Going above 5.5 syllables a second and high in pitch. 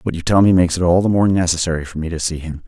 No: 7.4 syllables/s; very low, 85 Hz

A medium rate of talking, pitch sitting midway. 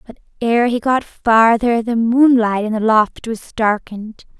No: average, 165 wpm; high, 230 Hz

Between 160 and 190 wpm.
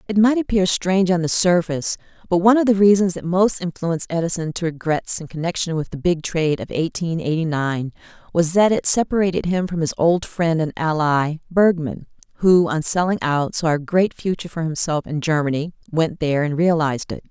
No: average, 200 wpm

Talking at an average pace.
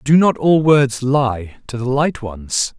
Yes: average, 195 wpm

